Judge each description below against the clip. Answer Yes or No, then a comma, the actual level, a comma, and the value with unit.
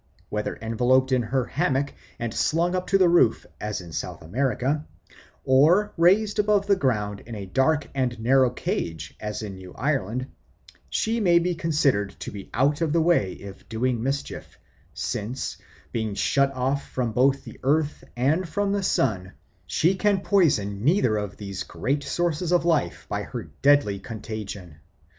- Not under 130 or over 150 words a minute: No, average, 165 wpm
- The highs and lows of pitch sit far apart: Yes, wide, 7.6 semitones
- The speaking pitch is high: No, low, 130 Hz